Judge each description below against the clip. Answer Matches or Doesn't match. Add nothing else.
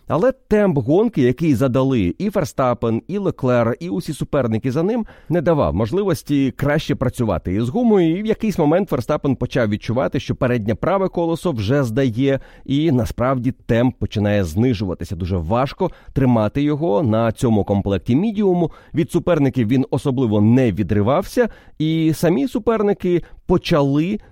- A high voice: Doesn't match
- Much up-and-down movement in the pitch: Matches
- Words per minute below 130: Doesn't match